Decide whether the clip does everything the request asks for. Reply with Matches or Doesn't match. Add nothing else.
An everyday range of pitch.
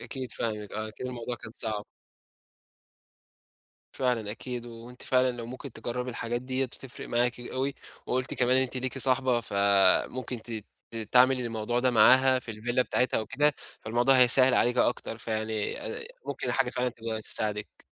Doesn't match